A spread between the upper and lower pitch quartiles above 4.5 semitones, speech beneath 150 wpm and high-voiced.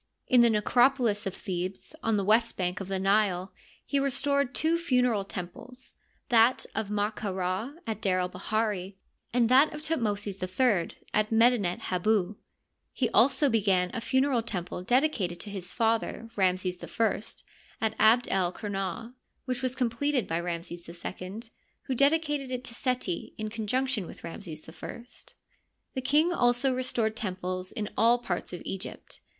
No: average, 5.0 semitones; average, 155 wpm; high, 220 Hz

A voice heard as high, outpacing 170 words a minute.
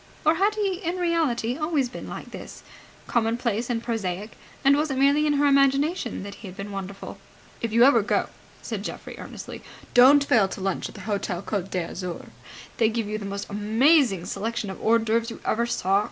Yes: high, 230 Hz; average, 195 wpm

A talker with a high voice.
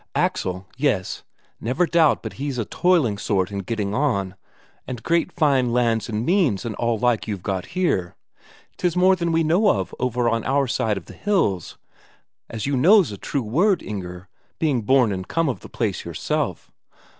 No: low, 125 Hz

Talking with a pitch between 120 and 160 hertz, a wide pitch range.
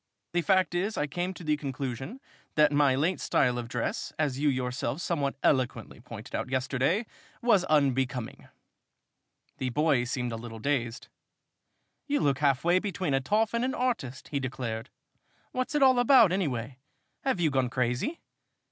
Yes: medium, 140 Hz; wide, 6.3 semitones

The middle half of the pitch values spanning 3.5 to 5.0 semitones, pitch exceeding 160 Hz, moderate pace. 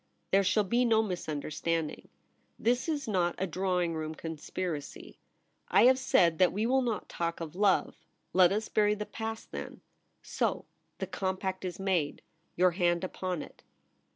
Yes: average, 3.8 semitones; medium, 185 Hz; average, 160 wpm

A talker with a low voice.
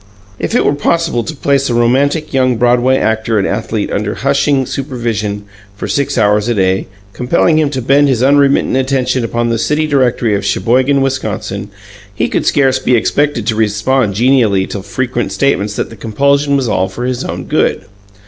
Yes: low, 125 Hz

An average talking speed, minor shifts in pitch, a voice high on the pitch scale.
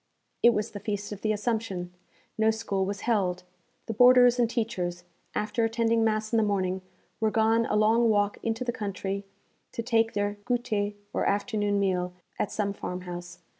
Yes: average, 170 wpm; narrow, 2.3 semitones; high, 215 Hz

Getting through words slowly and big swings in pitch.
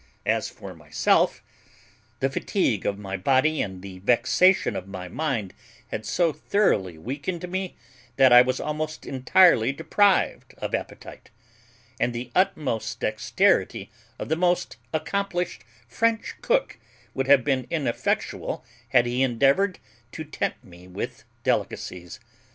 Yes: slow, 130 wpm; wide, 7.5 semitones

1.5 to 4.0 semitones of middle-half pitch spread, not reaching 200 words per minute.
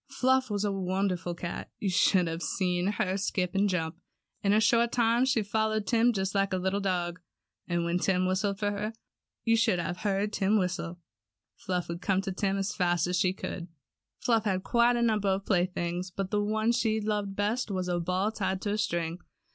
No: average, 3.0 semitones; fast, 205 wpm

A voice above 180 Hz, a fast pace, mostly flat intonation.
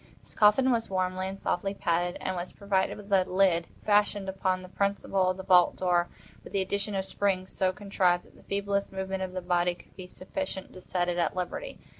Yes: high, 190 Hz; fast, 215 wpm; narrow, 1.6 semitones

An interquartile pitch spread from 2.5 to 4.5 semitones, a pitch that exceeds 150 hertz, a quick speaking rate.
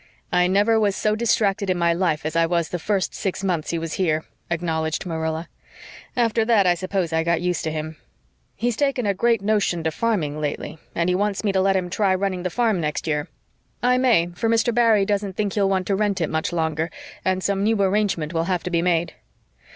Yes: average, 3.8 semitones; medium, 185 Hz; fast, 220 wpm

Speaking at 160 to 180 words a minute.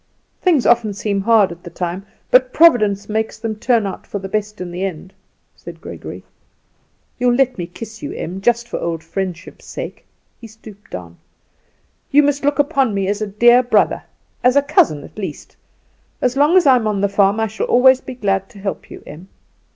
No: average, 200 wpm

